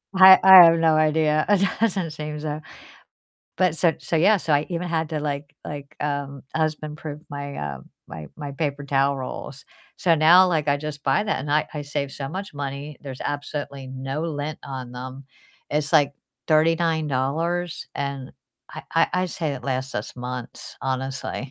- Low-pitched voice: No, medium, 150 Hz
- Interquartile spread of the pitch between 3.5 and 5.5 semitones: No, narrow, 2.6 semitones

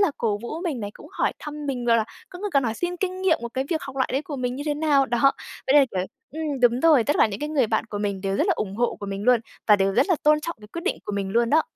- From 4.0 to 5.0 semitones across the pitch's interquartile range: No, wide, 5.6 semitones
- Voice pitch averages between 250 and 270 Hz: Yes, very high, 265 Hz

